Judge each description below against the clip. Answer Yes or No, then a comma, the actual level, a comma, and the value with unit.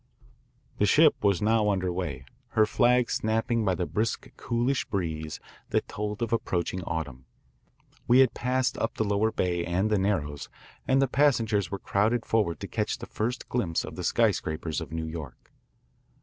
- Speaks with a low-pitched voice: Yes, low, 105 Hz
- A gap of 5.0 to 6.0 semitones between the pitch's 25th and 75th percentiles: Yes, average, 5.3 semitones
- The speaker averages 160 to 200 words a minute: Yes, average, 170 wpm